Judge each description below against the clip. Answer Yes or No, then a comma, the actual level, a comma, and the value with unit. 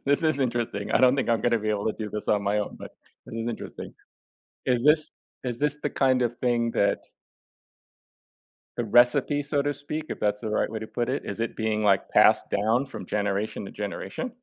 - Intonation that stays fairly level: No, average, 4.2 semitones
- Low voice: Yes, low, 115 Hz